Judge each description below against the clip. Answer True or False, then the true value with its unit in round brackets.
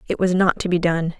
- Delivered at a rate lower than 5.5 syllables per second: False (5.7 syllables/s)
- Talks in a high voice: False (175 Hz)